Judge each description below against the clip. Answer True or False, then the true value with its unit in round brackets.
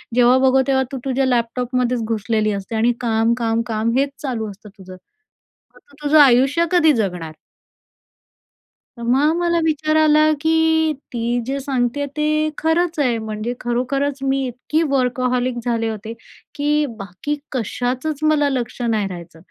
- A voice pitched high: True (250 Hz)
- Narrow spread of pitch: False (4.0 semitones)